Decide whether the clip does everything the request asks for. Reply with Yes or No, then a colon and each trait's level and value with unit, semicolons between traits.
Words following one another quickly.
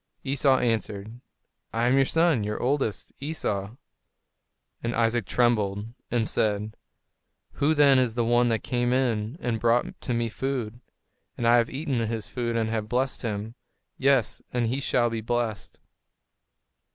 No: average, 155 wpm